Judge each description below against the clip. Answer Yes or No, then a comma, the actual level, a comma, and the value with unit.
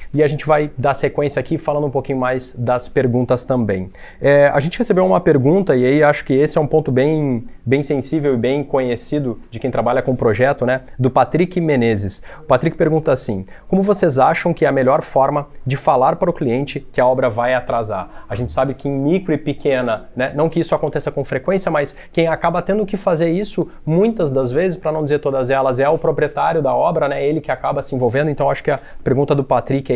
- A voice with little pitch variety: No, average, 3.3 semitones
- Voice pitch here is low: No, medium, 145 Hz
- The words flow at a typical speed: No, fast, 230 wpm